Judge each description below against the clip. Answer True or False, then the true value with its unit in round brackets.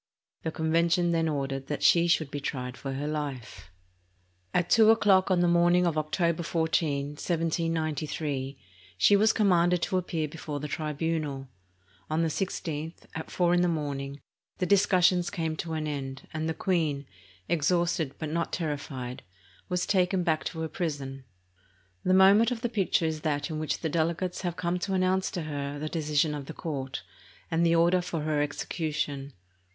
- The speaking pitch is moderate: True (160 Hz)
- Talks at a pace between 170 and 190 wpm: True (175 wpm)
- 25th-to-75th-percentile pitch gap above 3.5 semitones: False (3.1 semitones)